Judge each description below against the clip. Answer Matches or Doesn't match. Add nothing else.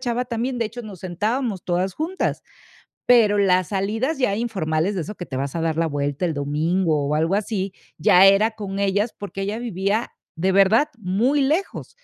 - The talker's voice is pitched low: Doesn't match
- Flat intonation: Doesn't match